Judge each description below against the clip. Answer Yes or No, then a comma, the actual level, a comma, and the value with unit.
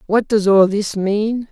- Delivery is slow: No, average, 200 wpm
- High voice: Yes, high, 205 Hz